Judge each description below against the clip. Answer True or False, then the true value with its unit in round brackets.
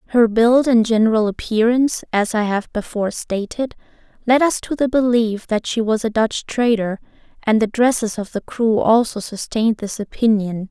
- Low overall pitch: False (225 Hz)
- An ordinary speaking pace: True (175 wpm)